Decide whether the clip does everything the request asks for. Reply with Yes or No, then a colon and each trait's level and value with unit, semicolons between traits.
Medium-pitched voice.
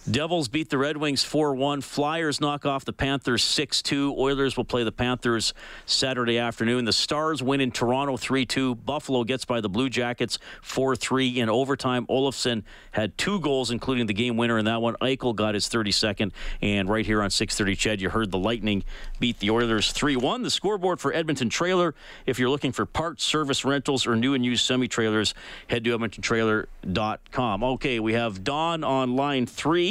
No: low, 125 Hz